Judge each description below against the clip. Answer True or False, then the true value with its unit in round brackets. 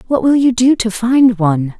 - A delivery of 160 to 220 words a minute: False (235 wpm)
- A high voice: True (230 Hz)